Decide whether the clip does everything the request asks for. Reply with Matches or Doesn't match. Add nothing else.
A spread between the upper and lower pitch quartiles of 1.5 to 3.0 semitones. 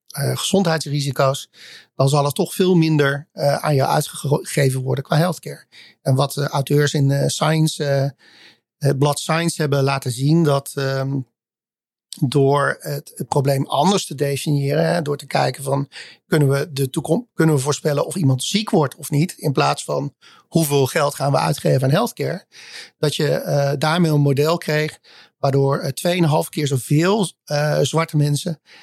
Matches